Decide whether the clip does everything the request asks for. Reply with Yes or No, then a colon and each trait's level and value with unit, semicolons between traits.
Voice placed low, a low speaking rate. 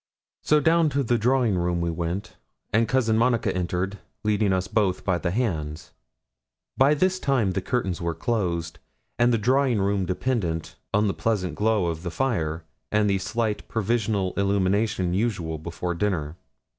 No: low, 100 Hz; average, 160 wpm